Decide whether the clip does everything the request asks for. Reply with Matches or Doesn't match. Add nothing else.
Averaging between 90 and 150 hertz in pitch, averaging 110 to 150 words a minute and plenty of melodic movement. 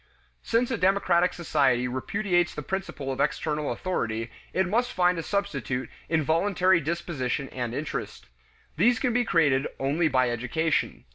Doesn't match